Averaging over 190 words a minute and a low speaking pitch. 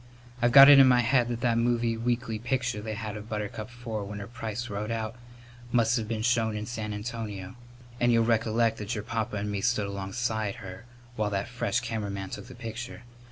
Yes: fast, 205 wpm; low, 115 Hz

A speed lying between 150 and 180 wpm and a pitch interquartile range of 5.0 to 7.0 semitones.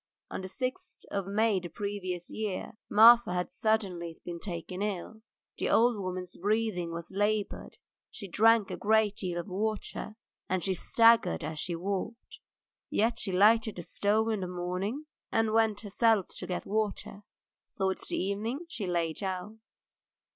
No: average, 160 wpm; average, 3.3 semitones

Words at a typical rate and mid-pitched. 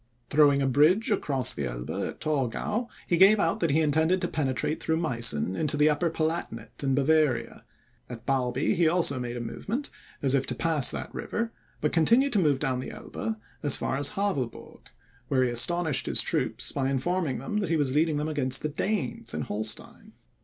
Yes: average, 195 wpm; medium, 150 Hz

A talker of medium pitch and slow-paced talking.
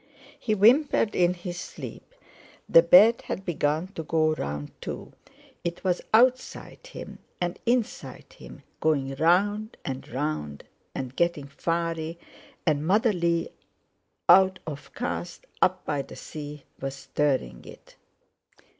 Yes: medium, 170 Hz; slow, 130 wpm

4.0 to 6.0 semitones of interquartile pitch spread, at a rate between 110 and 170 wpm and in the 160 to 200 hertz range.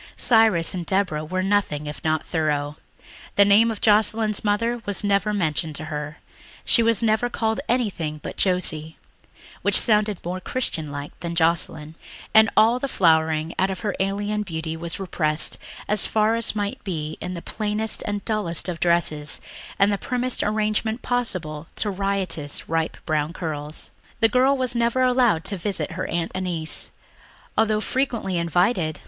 Yes: average, 5.1 semitones; average, 160 wpm; high, 190 Hz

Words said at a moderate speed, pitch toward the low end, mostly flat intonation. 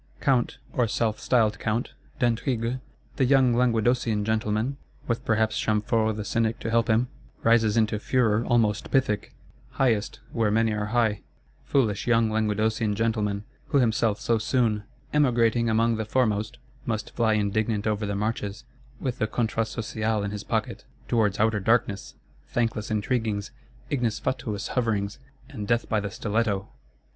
Yes: average, 145 wpm; low, 110 Hz; narrow, 1.8 semitones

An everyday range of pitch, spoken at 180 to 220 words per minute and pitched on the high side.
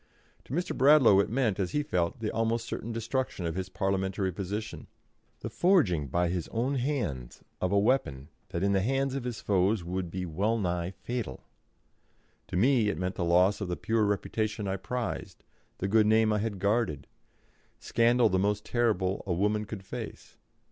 No: average, 4.0 semitones; average, 185 wpm; low, 105 Hz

